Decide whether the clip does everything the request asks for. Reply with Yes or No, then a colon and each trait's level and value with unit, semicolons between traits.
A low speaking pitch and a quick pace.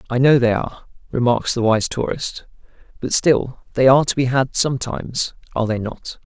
No: low, 125 Hz; average, 180 wpm